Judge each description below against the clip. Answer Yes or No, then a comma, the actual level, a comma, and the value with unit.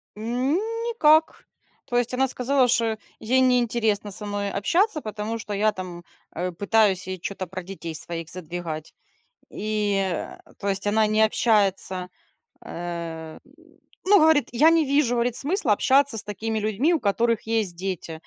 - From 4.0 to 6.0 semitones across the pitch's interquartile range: Yes, average, 5.0 semitones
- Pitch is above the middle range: Yes, high, 215 Hz